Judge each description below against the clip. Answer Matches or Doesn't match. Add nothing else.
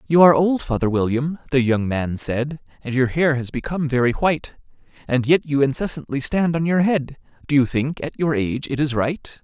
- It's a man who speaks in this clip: Matches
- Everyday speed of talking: Doesn't match